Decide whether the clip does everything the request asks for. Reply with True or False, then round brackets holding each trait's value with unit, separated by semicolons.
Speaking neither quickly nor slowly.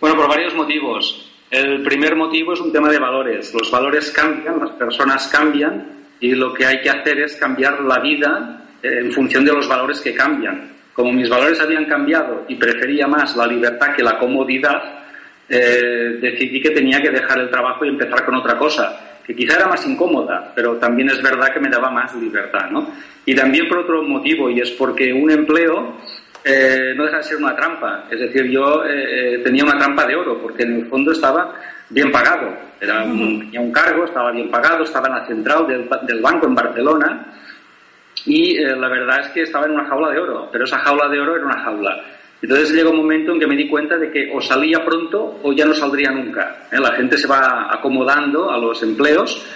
False (210 wpm)